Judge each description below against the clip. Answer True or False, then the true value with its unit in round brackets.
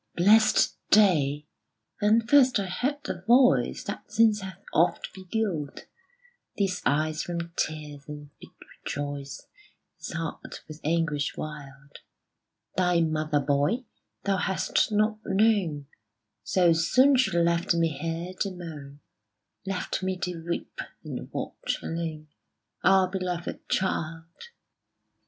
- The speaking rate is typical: False (120 wpm)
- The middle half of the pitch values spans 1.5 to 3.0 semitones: False (4.2 semitones)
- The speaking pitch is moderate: True (170 Hz)